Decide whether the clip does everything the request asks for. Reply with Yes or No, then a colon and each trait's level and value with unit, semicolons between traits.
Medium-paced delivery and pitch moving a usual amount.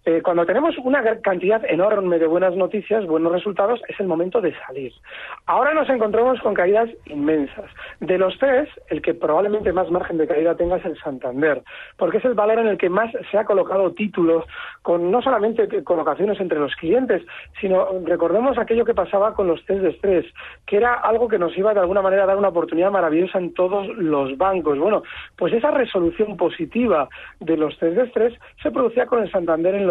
No: fast, 195 wpm; average, 4.5 semitones